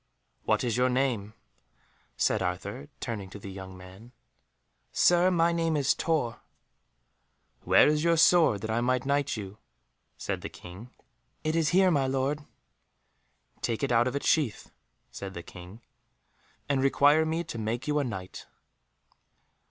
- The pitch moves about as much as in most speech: No, wide, 6.2 semitones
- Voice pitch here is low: Yes, low, 130 Hz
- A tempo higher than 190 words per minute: No, average, 150 wpm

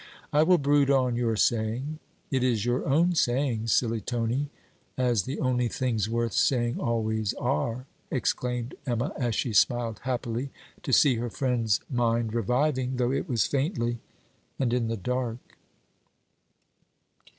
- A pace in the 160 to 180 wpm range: No, average, 140 wpm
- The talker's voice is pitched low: Yes, low, 120 Hz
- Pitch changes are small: Yes, narrow, 2.3 semitones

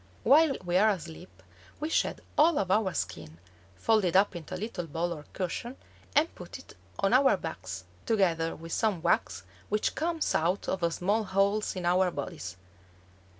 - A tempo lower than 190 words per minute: Yes, average, 170 wpm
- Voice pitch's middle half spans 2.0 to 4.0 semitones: No, average, 4.7 semitones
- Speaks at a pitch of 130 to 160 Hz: No, high, 190 Hz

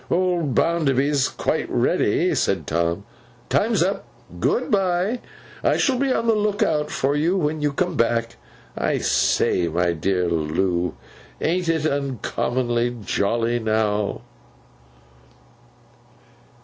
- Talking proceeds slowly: Yes, slow, 120 wpm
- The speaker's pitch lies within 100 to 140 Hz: Yes, low, 135 Hz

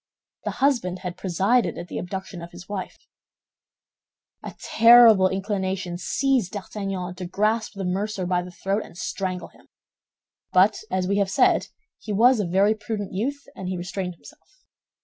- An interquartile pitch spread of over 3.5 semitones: No, average, 2.9 semitones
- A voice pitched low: No, high, 195 Hz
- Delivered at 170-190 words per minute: No, average, 160 wpm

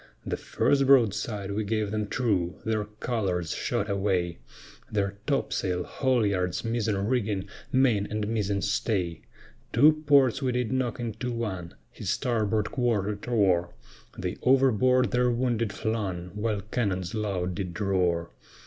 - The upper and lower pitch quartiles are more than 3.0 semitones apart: Yes, average, 3.7 semitones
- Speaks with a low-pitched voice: Yes, low, 105 Hz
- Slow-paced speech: Yes, slow, 130 wpm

